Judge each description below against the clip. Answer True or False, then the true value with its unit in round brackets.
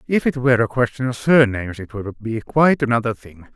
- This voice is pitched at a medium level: False (120 Hz)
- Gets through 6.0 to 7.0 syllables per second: True (6.1 syllables/s)